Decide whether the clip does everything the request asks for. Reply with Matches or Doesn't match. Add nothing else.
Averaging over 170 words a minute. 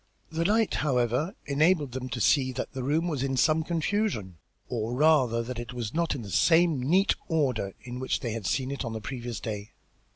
Matches